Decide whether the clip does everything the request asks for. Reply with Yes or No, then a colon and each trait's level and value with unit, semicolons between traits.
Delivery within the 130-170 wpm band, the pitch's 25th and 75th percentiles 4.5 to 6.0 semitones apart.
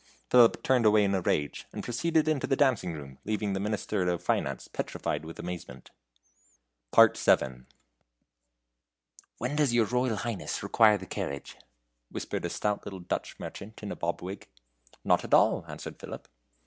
Yes: average, 160 wpm; average, 5.3 semitones